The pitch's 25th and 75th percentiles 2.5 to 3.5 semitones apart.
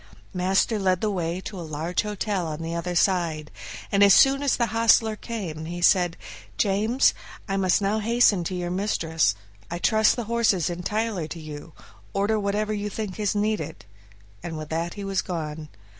No: average, 4.1 semitones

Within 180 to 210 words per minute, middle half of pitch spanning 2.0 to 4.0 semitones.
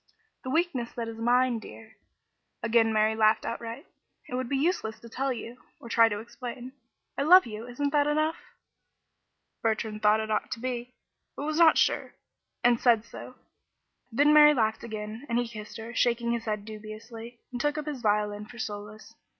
Yes: average, 185 wpm; average, 2.7 semitones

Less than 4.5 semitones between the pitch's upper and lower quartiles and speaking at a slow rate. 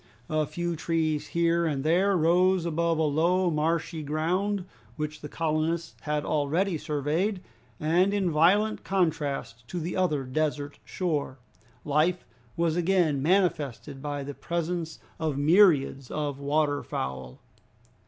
Yes: average, 2.9 semitones; slow, 130 wpm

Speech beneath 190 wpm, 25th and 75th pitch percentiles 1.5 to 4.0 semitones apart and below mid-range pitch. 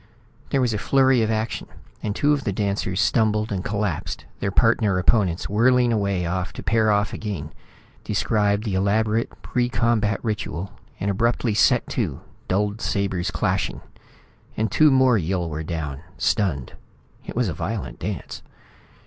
Yes: average, 150 wpm; average, 3.2 semitones; low, 105 Hz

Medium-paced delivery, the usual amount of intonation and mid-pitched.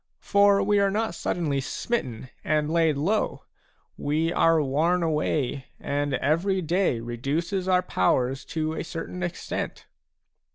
No: slow, 130 wpm; average, 4.4 semitones; medium, 160 Hz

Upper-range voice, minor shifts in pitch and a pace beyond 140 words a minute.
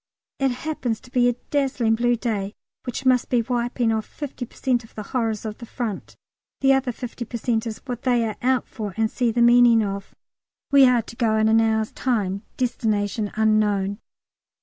Yes: high, 235 Hz; narrow, 2.3 semitones; average, 200 wpm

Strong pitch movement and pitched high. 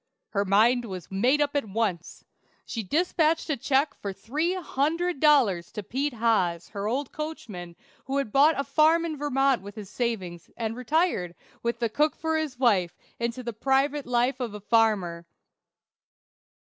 Yes: wide, 6.1 semitones; high, 240 Hz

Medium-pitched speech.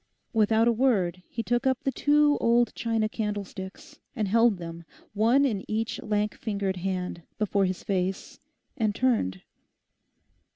No: high, 215 Hz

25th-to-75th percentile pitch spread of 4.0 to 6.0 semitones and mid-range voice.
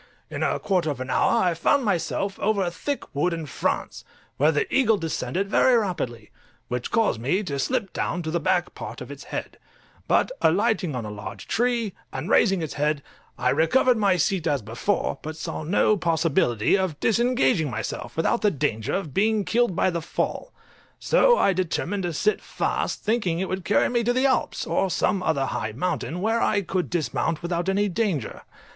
Yes: wide, 5.5 semitones; medium, 180 Hz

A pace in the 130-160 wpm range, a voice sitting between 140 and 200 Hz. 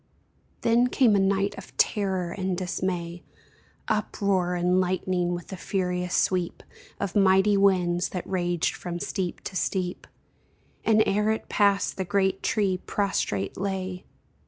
Yes: slow, 135 wpm; high, 190 Hz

